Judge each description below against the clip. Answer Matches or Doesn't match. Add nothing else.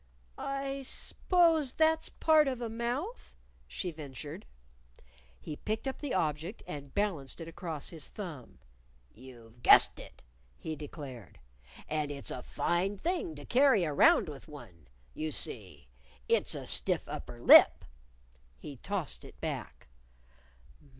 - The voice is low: Doesn't match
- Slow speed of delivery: Matches